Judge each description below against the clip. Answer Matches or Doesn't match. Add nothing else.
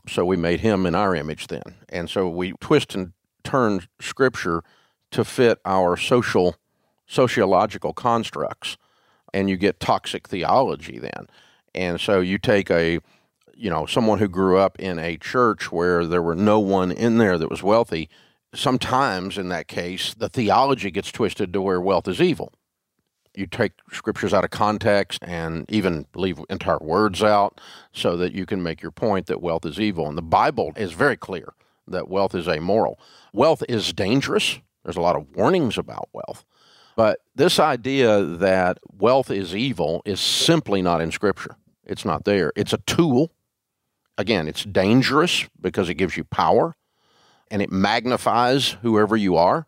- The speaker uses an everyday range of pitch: Matches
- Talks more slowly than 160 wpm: Doesn't match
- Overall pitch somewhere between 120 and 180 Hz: Doesn't match